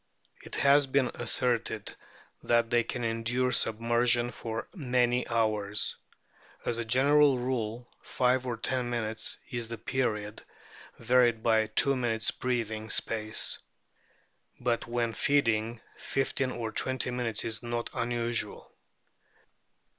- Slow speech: Yes, slow, 120 wpm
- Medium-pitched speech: No, low, 120 Hz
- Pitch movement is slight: Yes, narrow, 1.9 semitones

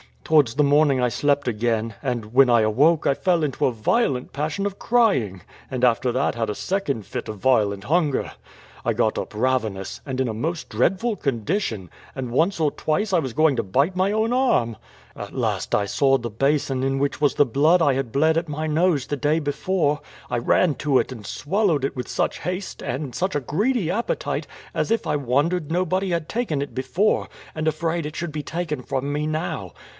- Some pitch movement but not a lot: Yes, average, 5.0 semitones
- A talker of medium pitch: Yes, medium, 145 Hz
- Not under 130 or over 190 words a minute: No, fast, 205 wpm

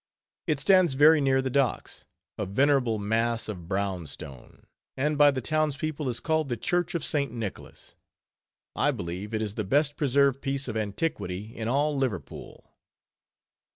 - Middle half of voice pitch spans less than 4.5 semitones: No, wide, 5.4 semitones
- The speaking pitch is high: No, low, 130 Hz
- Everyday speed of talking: Yes, average, 160 wpm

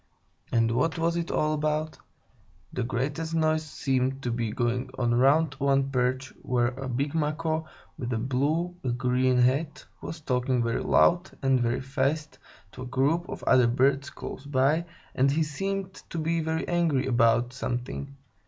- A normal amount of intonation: Yes, average, 3.9 semitones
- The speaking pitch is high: No, low, 135 Hz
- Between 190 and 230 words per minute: No, average, 165 wpm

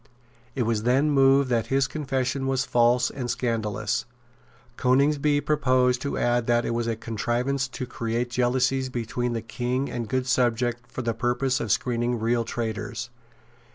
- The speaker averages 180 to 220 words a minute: No, average, 155 wpm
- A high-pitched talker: No, low, 125 Hz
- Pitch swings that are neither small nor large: No, narrow, 1.9 semitones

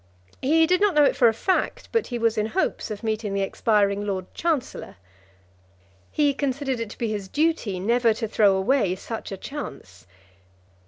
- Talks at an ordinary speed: Yes, average, 180 wpm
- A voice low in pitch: No, high, 230 Hz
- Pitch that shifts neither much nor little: No, wide, 5.8 semitones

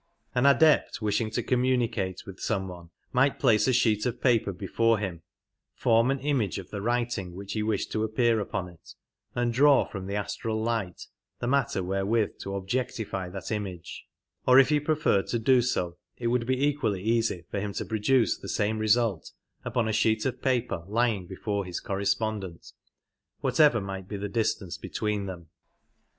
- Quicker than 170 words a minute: Yes, average, 180 wpm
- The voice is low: Yes, low, 110 Hz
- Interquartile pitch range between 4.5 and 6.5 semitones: No, average, 3.8 semitones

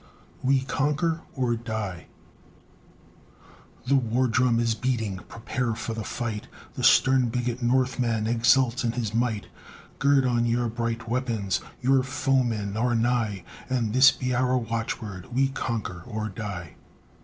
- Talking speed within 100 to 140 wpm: Yes, slow, 135 wpm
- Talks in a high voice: No, low, 120 Hz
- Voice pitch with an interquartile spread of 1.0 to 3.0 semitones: Yes, narrow, 2.5 semitones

